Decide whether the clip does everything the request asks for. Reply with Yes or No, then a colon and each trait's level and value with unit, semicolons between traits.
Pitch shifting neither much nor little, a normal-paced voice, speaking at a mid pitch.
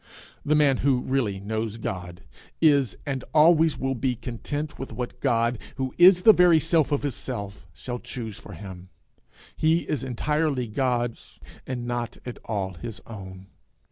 No: average, 4.9 semitones; average, 160 wpm; low, 125 Hz